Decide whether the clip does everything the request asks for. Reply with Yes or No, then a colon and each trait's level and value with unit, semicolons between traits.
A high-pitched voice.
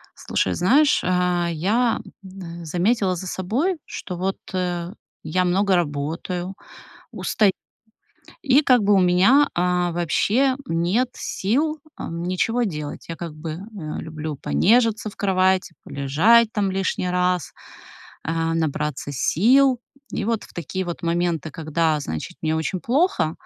No: medium, 180 Hz